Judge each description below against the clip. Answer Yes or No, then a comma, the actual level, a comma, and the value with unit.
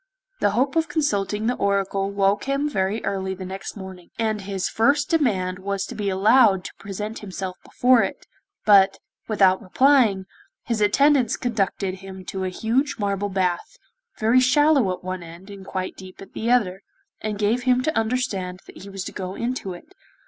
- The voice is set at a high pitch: Yes, high, 200 Hz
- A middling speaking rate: Yes, average, 180 wpm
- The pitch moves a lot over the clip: No, average, 4.3 semitones